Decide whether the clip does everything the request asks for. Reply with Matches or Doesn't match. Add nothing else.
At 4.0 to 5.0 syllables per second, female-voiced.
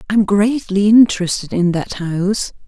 Matches